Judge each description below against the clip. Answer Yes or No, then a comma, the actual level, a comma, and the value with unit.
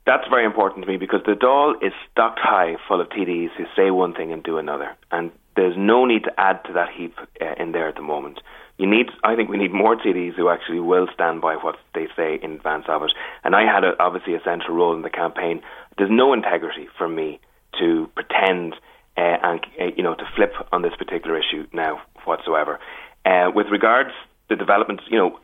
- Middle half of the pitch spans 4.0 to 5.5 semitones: No, narrow, 2.6 semitones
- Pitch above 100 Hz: No, very low, 90 Hz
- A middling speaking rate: No, fast, 225 wpm